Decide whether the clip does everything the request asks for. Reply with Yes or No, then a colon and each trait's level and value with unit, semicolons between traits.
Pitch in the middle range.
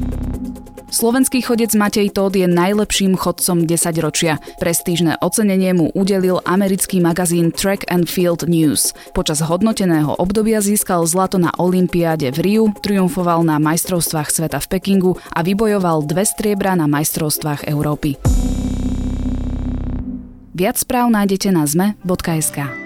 Yes: medium, 175 Hz